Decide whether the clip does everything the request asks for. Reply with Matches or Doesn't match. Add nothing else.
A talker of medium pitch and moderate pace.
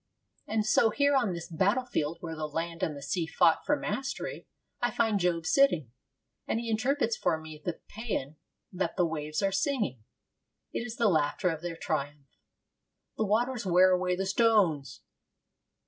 Matches